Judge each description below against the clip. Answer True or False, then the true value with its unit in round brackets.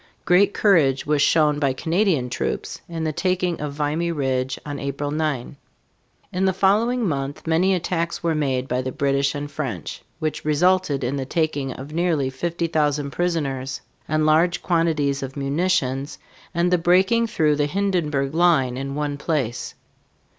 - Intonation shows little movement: False (3.9 semitones)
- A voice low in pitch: False (150 Hz)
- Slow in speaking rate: False (155 wpm)